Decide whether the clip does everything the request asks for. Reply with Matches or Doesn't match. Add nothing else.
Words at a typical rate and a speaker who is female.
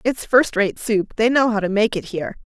Doesn't match